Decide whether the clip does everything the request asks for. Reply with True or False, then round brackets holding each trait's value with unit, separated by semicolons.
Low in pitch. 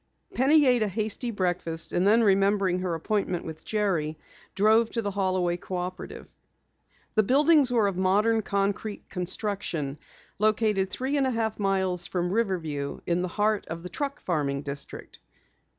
False (195 Hz)